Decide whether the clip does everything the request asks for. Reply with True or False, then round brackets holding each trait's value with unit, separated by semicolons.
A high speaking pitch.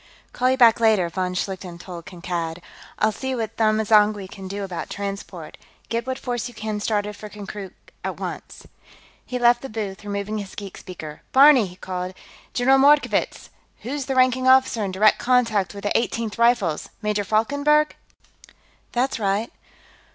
True (215 Hz)